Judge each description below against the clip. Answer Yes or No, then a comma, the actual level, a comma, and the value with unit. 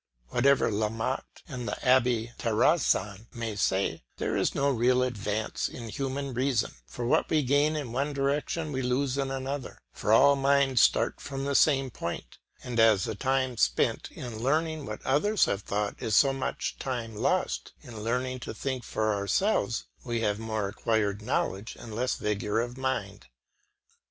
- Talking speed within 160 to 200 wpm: Yes, average, 170 wpm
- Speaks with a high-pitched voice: No, low, 125 Hz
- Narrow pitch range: No, average, 3.8 semitones